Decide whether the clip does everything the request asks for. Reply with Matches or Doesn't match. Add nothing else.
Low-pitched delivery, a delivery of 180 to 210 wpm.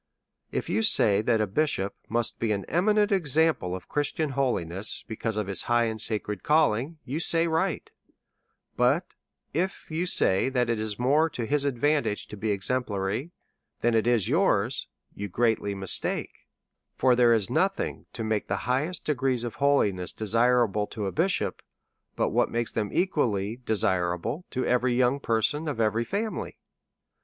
Doesn't match